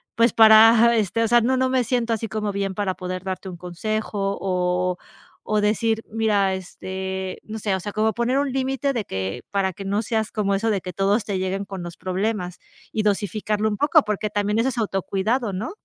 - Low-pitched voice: No, high, 210 Hz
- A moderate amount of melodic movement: Yes, average, 3.0 semitones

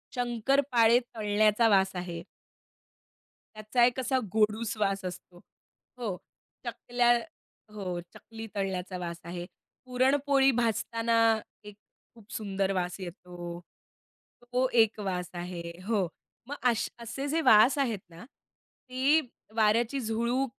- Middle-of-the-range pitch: No, high, 220 Hz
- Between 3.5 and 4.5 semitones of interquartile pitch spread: Yes, average, 4.2 semitones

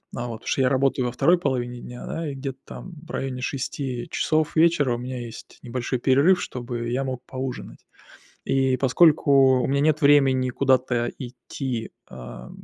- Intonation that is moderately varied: No, narrow, 2.3 semitones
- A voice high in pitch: No, low, 130 Hz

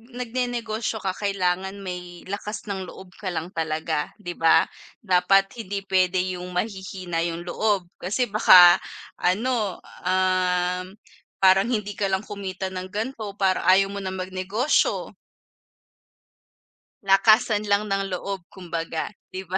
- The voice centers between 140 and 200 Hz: Yes, high, 190 Hz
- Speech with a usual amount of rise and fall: No, narrow, 2.3 semitones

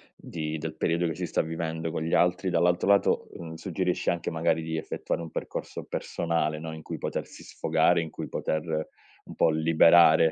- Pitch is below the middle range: Yes, very low, 80 Hz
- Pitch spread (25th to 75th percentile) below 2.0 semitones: Yes, narrow, 1.3 semitones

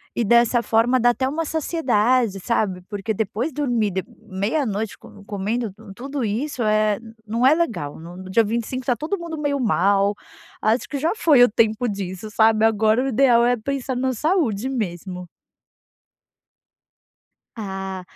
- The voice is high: Yes, high, 230 Hz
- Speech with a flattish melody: No, average, 4.2 semitones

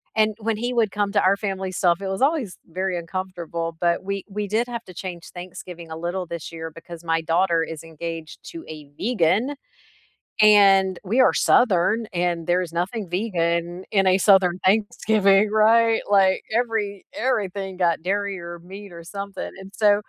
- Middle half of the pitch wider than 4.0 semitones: No, average, 3.3 semitones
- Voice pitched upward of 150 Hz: Yes, high, 190 Hz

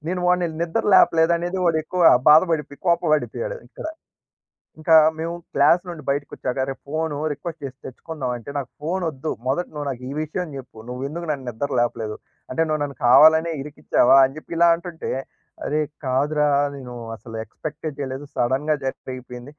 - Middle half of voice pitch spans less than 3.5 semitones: No, average, 3.8 semitones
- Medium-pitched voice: Yes, medium, 150 Hz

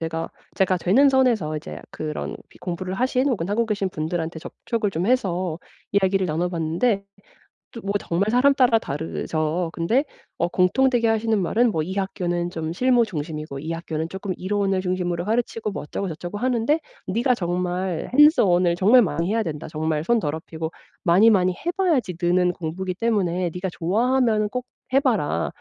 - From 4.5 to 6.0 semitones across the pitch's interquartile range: Yes, average, 5.2 semitones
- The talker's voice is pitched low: No, medium, 185 Hz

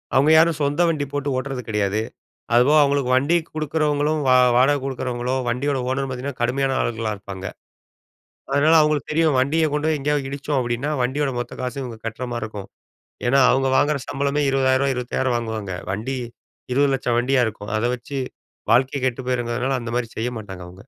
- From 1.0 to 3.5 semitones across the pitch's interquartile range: Yes, average, 3.0 semitones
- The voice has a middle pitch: No, low, 130 Hz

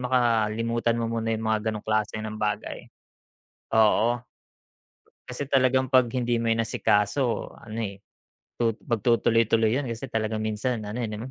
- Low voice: Yes, low, 115 Hz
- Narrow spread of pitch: Yes, narrow, 2.0 semitones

